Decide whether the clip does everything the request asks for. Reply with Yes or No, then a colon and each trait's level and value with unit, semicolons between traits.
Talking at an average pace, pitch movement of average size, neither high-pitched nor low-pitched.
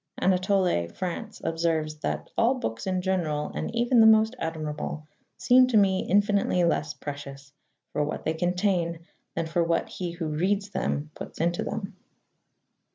Yes: average, 150 wpm; average, 4.3 semitones; medium, 175 Hz